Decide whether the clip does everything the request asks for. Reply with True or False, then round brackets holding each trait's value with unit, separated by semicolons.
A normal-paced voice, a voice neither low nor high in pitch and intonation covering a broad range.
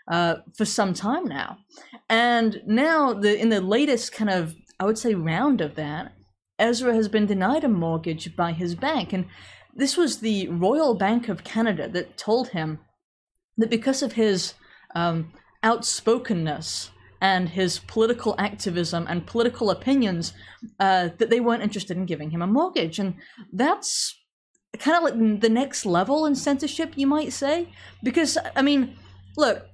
False (160 wpm; 215 Hz; 6.2 semitones)